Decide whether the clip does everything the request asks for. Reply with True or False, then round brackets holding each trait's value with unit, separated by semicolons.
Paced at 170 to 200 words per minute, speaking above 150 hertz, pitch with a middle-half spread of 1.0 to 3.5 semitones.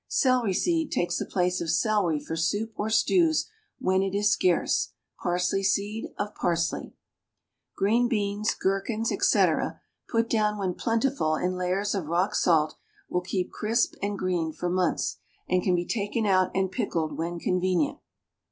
False (155 wpm; 190 Hz; 3.1 semitones)